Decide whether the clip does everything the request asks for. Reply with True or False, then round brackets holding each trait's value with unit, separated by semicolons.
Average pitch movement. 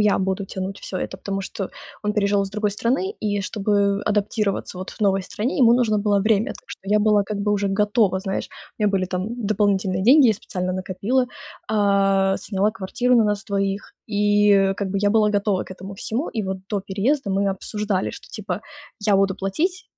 False (1.6 semitones)